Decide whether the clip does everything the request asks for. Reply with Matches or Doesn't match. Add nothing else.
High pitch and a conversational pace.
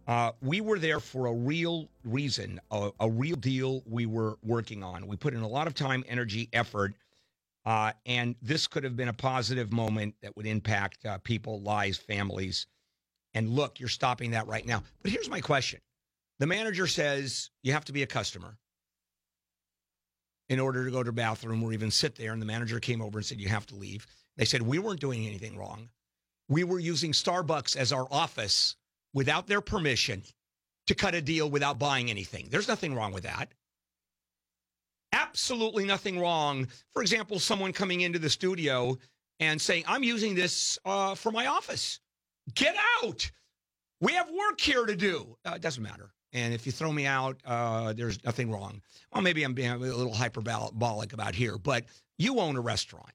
Doesn't match